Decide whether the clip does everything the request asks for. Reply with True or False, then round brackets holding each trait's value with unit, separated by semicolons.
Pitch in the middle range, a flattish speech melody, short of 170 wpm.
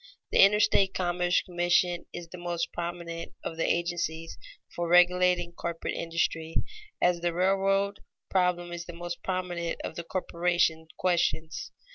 True (175 Hz; 1.1 semitones; 140 wpm)